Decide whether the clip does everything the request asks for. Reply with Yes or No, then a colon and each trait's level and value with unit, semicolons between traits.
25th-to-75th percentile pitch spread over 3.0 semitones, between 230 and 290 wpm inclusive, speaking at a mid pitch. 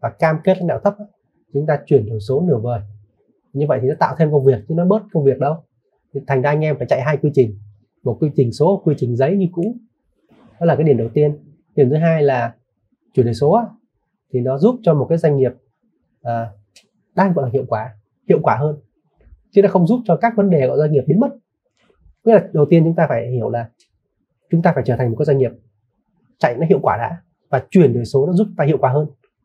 Yes: average, 5.3 semitones; average, 245 wpm; medium, 150 Hz